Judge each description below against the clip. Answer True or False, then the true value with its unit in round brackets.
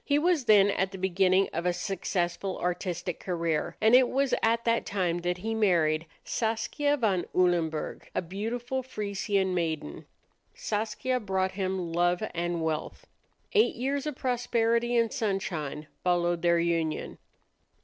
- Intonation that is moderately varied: True (4.9 semitones)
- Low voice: False (190 Hz)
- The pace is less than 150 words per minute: True (140 wpm)